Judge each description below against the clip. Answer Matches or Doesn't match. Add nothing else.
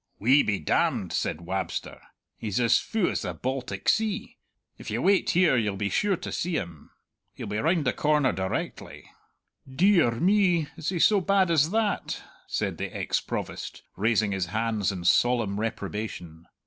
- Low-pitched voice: Matches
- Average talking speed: Matches